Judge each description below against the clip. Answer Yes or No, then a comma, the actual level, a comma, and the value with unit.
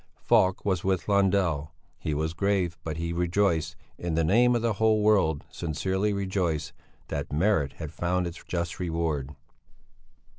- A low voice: Yes, very low, 85 Hz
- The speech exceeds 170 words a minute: No, average, 150 wpm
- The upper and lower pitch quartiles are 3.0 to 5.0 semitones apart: Yes, average, 3.6 semitones